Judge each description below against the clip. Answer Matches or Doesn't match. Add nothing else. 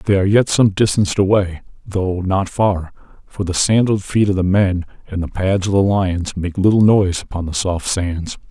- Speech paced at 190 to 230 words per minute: Matches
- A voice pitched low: Matches